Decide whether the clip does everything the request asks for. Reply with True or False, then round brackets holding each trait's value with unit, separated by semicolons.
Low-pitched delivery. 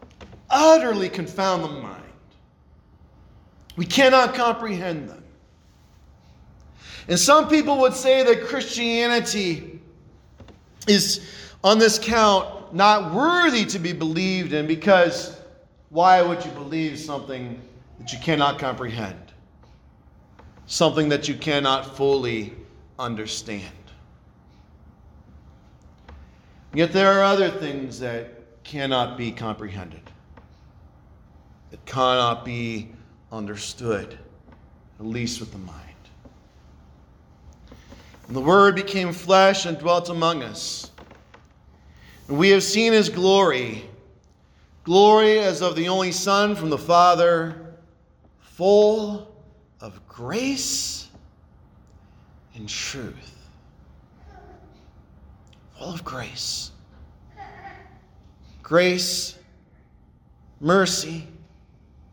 False (150 Hz)